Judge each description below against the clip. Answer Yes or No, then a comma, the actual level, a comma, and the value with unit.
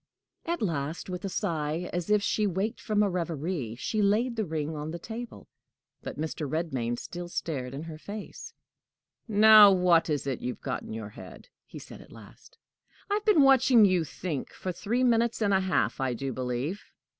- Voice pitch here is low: No, medium, 175 Hz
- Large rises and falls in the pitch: Yes, wide, 6.0 semitones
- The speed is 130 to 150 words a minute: No, average, 190 wpm